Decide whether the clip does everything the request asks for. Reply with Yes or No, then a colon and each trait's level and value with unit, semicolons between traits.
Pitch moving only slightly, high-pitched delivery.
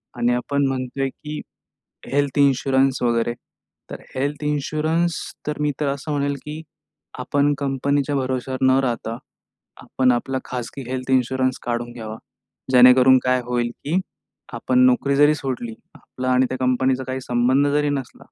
No: narrow, 2.1 semitones; low, 130 Hz